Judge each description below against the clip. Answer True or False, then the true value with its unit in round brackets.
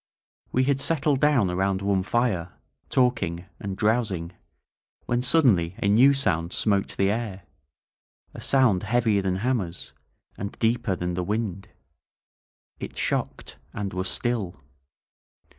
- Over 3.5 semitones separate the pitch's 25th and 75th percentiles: True (4.7 semitones)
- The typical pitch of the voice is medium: False (100 Hz)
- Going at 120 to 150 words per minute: True (135 wpm)